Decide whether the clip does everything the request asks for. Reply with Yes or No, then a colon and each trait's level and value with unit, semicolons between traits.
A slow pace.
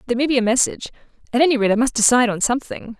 No: fast, 240 wpm